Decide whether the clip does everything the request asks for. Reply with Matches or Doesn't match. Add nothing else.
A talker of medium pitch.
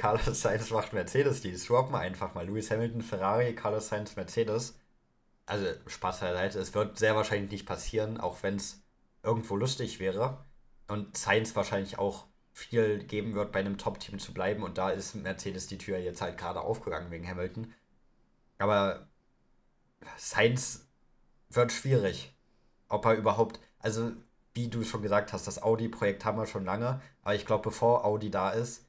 Doesn't match